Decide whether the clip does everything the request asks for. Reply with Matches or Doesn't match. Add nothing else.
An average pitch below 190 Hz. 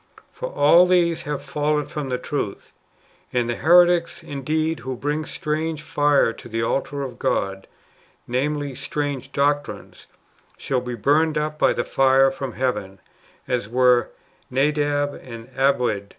Matches